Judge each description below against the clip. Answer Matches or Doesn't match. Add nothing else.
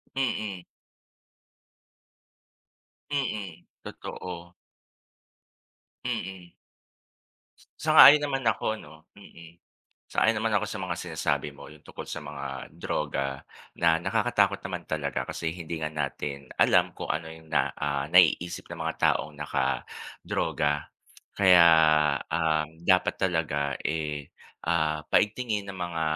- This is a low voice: Matches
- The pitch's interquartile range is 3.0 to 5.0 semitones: Matches